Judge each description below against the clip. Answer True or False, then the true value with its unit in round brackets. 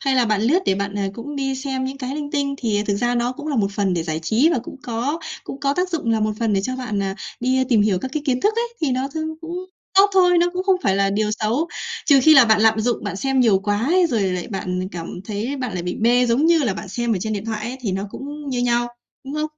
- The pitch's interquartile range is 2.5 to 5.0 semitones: False (5.4 semitones)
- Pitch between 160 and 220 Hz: False (245 Hz)